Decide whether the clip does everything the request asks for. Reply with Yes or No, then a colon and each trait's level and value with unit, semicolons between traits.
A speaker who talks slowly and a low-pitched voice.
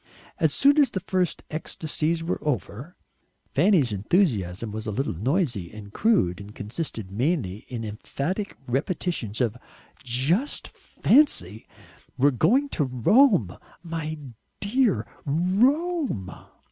No: slow, 115 wpm; medium, 150 Hz